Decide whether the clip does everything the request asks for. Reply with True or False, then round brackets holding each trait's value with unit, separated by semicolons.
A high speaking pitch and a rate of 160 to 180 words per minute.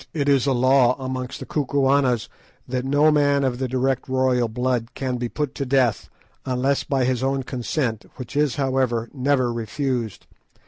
False (130 Hz; 170 wpm)